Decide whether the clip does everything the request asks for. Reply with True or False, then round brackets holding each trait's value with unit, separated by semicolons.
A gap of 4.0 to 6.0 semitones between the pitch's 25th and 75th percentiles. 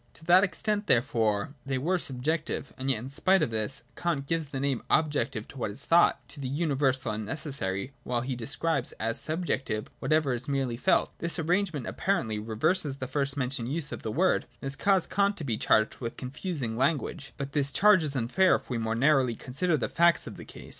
True (5.2 semitones)